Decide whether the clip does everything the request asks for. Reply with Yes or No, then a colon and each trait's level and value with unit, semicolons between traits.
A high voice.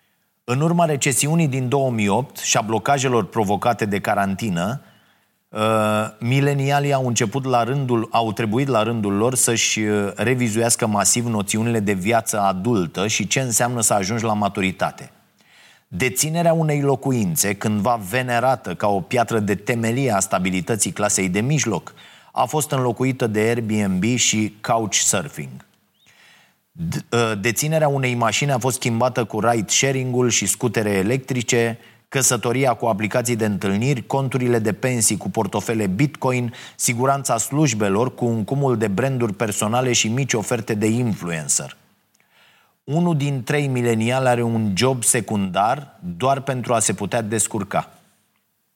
No: low, 120 Hz